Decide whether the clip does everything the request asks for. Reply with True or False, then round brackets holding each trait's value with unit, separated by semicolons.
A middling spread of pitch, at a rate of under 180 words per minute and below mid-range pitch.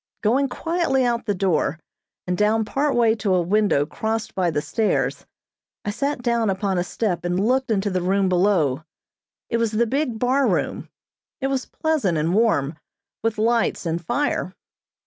False (4.9 semitones; 170 wpm; 215 Hz)